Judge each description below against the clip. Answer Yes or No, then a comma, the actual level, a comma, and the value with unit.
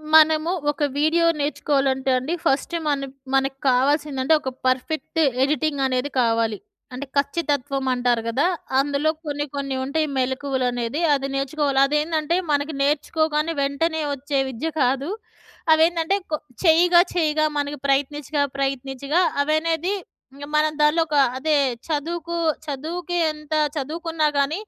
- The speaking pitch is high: Yes, very high, 290 Hz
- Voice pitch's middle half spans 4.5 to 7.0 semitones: No, narrow, 2.6 semitones